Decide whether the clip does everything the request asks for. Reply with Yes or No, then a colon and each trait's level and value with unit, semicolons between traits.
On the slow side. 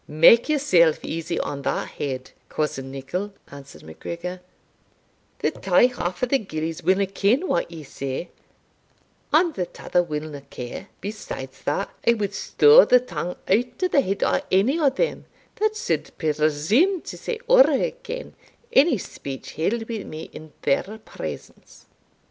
No: average, 150 wpm